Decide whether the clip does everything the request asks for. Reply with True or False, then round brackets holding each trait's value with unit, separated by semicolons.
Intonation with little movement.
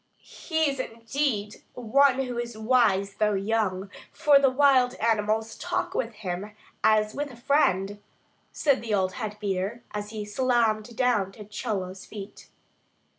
False (3.6 semitones)